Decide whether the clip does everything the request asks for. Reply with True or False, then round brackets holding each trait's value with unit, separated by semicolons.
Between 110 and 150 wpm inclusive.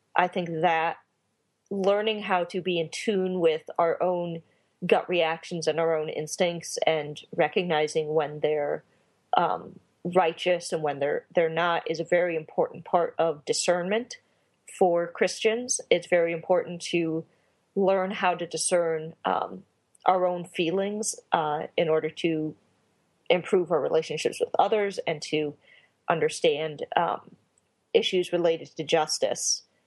True (135 wpm)